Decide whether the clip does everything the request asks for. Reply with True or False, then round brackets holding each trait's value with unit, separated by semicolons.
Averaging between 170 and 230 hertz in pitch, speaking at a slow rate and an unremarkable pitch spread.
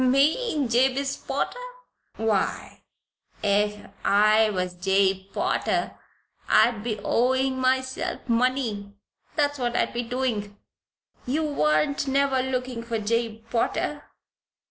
False (240 Hz; 105 wpm; 4.1 semitones)